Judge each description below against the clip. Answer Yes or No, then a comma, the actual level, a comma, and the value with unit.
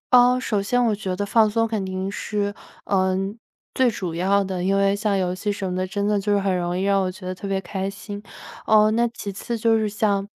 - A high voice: Yes, high, 200 Hz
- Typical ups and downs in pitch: No, narrow, 2.1 semitones